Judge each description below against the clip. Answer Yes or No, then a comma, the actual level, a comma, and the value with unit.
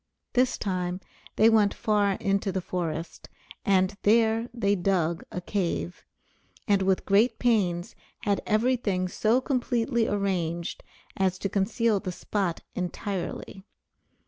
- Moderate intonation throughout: Yes, average, 3.2 semitones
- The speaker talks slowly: Yes, slow, 125 wpm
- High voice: Yes, high, 200 Hz